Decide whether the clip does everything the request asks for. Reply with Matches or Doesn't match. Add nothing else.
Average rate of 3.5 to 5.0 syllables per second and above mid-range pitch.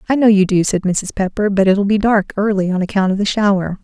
Doesn't match